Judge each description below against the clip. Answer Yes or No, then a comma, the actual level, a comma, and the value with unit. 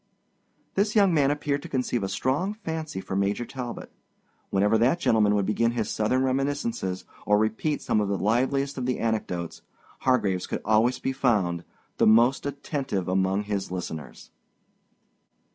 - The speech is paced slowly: No, average, 155 wpm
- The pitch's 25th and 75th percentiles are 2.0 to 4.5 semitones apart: No, wide, 5.4 semitones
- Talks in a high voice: No, low, 115 Hz